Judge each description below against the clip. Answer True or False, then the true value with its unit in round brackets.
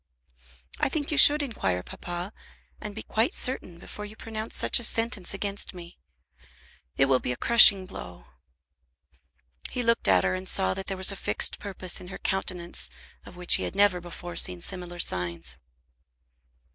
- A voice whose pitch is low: False (185 Hz)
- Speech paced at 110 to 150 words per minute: False (170 wpm)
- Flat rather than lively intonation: False (4.3 semitones)